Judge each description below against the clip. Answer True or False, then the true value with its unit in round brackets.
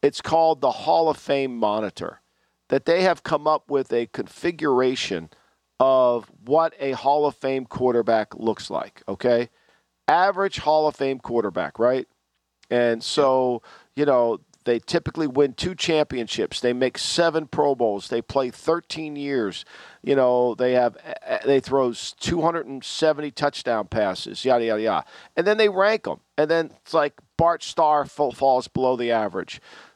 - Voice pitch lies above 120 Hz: True (135 Hz)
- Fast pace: False (150 wpm)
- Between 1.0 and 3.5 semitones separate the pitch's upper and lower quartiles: False (4.3 semitones)